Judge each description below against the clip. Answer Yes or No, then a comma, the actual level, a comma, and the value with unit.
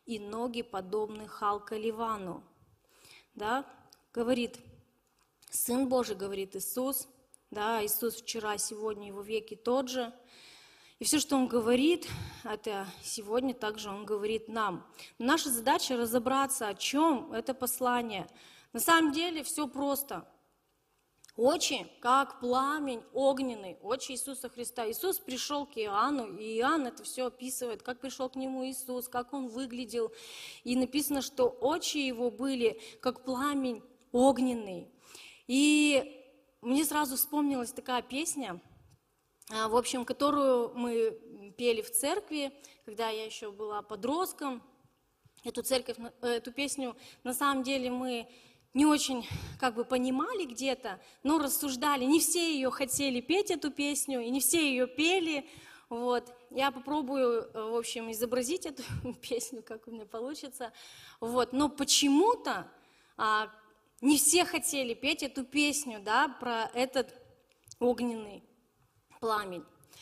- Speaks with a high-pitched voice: Yes, very high, 250 Hz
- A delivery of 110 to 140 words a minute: Yes, average, 130 wpm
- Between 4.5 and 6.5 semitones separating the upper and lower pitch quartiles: No, average, 3.3 semitones